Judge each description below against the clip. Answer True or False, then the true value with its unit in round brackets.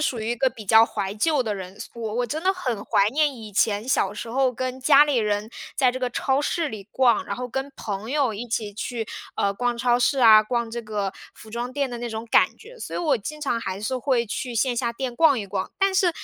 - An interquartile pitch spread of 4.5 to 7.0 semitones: False (3.6 semitones)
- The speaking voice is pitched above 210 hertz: True (240 Hz)